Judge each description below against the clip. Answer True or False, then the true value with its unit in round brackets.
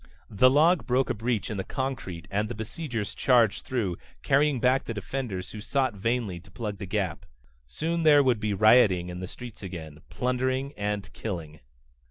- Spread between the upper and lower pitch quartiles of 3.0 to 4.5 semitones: False (5.2 semitones)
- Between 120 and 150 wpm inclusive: False (180 wpm)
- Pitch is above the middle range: False (110 Hz)